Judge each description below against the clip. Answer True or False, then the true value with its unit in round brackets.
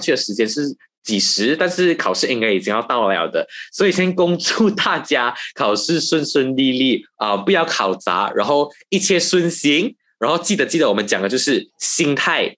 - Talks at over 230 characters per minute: True (275 characters per minute)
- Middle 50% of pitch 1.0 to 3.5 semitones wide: False (5.4 semitones)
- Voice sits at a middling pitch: True (160 Hz)